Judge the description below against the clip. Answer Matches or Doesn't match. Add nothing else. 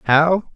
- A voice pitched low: Doesn't match